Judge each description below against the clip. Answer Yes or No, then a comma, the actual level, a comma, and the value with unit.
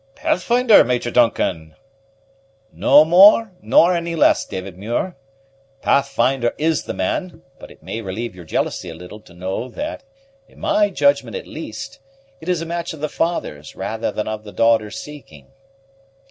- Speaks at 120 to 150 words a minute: No, average, 160 wpm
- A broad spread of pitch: Yes, wide, 8.7 semitones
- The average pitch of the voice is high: No, low, 135 Hz